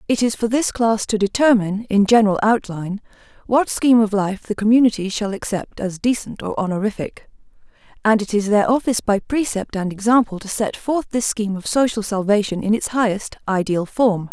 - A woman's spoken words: Yes, female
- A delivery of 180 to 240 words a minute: Yes, average, 185 wpm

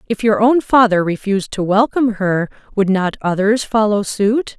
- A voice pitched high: Yes, high, 210 Hz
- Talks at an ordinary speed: Yes, average, 170 wpm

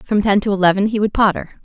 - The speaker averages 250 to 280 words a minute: Yes, fast, 255 wpm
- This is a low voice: No, high, 200 Hz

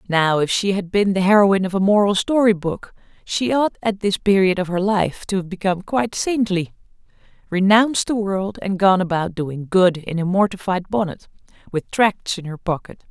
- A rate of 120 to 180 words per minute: No, average, 190 wpm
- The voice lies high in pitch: Yes, high, 195 Hz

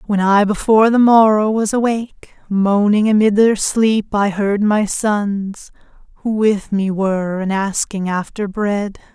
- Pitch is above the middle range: Yes, high, 205 Hz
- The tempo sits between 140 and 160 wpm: Yes, average, 150 wpm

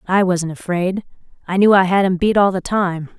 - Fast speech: Yes, fast, 225 wpm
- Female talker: Yes, female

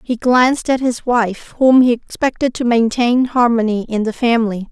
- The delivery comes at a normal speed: Yes, average, 180 wpm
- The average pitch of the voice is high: Yes, high, 240 Hz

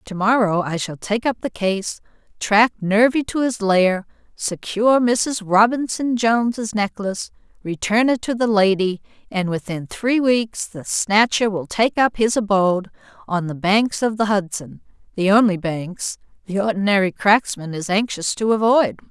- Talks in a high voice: Yes, high, 210 Hz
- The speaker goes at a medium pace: Yes, average, 155 wpm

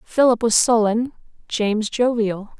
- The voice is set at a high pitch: Yes, high, 225 Hz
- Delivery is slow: Yes, slow, 115 wpm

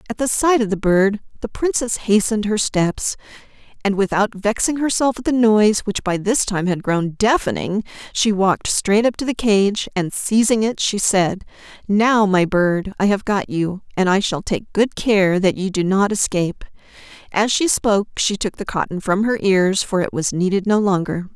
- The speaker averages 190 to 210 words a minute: Yes, average, 200 wpm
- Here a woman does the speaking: Yes, female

